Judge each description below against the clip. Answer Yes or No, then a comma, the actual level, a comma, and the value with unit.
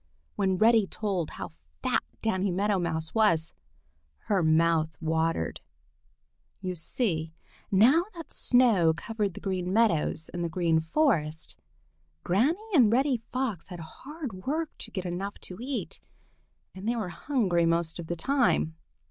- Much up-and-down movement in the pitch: Yes, wide, 5.7 semitones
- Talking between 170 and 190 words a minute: No, average, 140 wpm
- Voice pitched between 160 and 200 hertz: Yes, medium, 185 Hz